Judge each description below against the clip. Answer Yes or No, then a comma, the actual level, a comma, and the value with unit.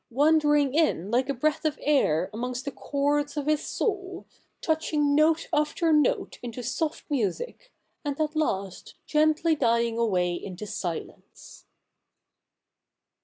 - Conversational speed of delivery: No, slow, 125 wpm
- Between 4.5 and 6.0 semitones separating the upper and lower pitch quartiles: Yes, average, 4.8 semitones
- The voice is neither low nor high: No, very high, 290 Hz